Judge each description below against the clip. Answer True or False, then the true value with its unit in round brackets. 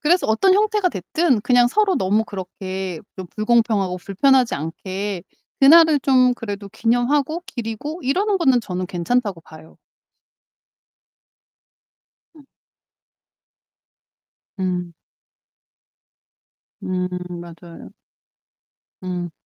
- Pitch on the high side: True (220 Hz)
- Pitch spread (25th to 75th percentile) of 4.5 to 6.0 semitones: False (7.0 semitones)